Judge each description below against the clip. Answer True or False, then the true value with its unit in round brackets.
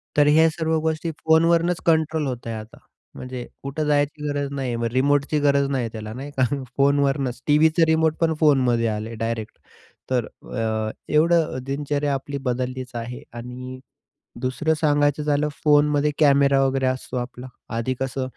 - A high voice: False (140 Hz)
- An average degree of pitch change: True (3.0 semitones)